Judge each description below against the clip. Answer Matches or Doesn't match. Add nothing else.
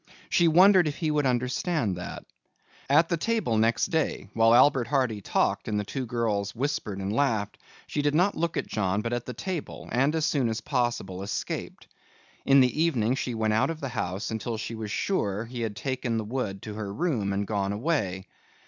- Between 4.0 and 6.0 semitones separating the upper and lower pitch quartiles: Matches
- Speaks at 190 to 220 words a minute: Matches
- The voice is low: Matches